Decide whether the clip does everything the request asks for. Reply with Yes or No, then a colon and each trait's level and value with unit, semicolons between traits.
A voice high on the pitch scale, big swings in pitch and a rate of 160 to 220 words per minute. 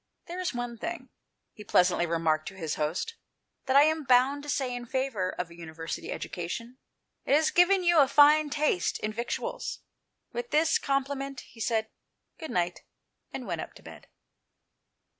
Yes: very high, 255 Hz; wide, 8.5 semitones; average, 180 wpm